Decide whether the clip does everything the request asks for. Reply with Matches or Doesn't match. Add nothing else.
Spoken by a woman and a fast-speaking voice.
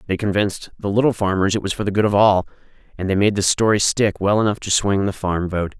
Doesn't match